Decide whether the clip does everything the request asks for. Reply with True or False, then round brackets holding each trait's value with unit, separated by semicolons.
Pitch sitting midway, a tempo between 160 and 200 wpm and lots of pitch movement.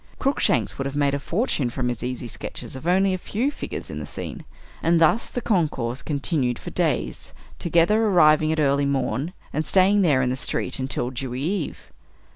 True (150 Hz; 190 wpm; 5.7 semitones)